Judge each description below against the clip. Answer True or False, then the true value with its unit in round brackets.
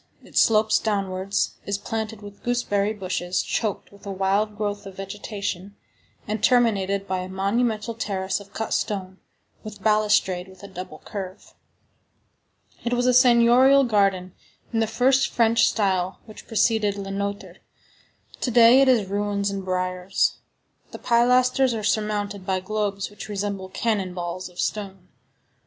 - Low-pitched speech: False (205 Hz)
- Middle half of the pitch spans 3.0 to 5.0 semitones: False (2.6 semitones)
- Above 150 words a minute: False (145 wpm)